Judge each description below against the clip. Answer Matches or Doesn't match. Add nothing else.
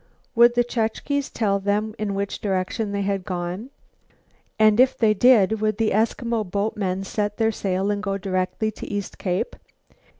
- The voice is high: Matches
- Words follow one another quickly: Doesn't match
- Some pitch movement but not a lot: Doesn't match